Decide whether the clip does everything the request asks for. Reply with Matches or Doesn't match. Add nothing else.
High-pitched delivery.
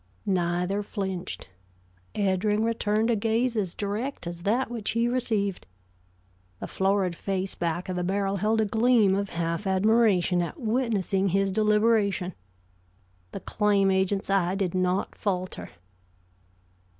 Matches